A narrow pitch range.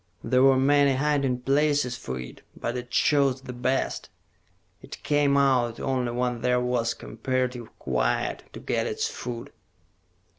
Yes: narrow, 2.1 semitones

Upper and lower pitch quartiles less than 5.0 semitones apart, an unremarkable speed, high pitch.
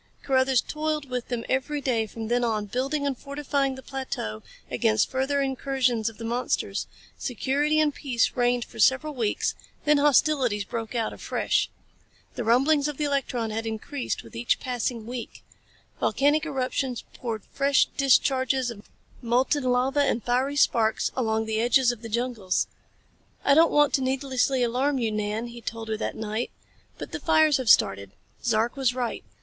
Yes: average, 3.3 semitones; average, 165 wpm; very high, 255 Hz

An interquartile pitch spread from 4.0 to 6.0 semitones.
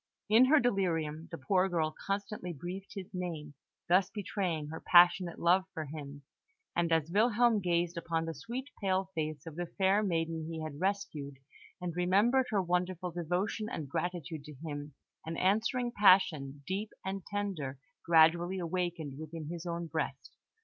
No: average, 3.5 semitones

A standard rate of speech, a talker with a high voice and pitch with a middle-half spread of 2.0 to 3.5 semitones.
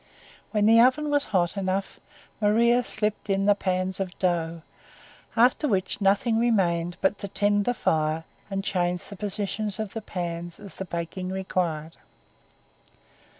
Yes: average, 150 wpm; high, 195 Hz; average, 3.2 semitones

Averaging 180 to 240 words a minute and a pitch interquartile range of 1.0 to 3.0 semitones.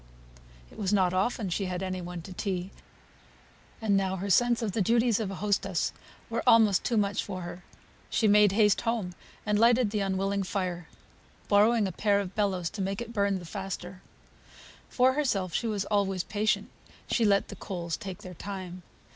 Yes: average, 185 wpm; narrow, 2.6 semitones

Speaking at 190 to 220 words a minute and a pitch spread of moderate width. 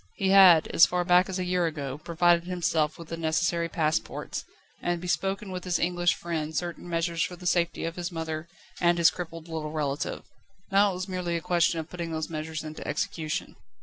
No: average, 200 wpm; narrow, 1.9 semitones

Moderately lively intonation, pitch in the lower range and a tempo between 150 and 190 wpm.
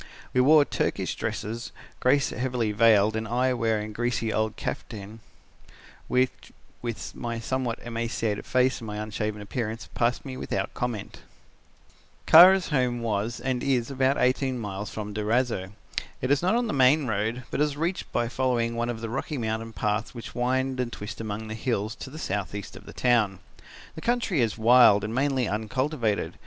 Yes: average, 3.1 semitones; low, 120 Hz; average, 175 wpm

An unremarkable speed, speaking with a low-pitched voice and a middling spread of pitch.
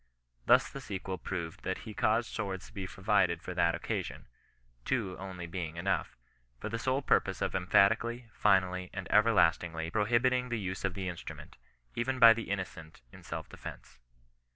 Yes: average, 170 wpm; very low, 95 Hz; average, 3.9 semitones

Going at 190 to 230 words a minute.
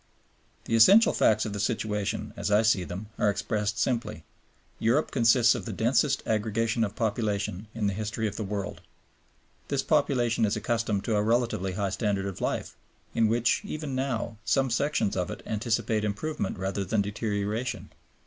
No: average, 170 wpm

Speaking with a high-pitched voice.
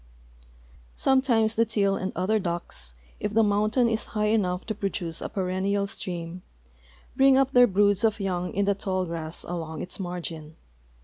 Yes: high, 195 Hz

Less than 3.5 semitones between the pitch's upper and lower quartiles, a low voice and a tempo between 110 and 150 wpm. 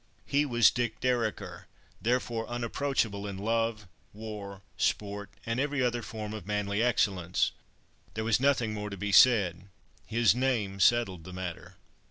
Yes: average, 3.1 semitones; low, 110 Hz; average, 145 wpm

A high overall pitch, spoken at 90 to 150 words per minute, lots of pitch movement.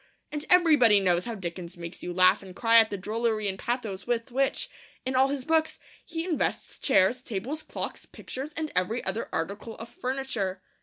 No: high, 230 Hz; average, 185 wpm; wide, 5.7 semitones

